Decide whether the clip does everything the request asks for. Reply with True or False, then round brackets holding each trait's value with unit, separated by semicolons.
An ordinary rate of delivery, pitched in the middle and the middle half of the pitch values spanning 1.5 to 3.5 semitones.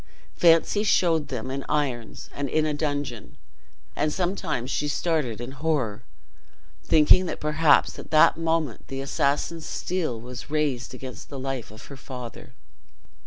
False (145 wpm; 145 Hz; 3.9 semitones)